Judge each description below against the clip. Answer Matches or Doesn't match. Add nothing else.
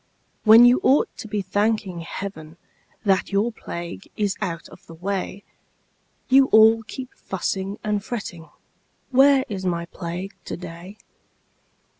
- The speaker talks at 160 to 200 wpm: Doesn't match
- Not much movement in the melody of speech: Doesn't match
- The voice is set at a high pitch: Matches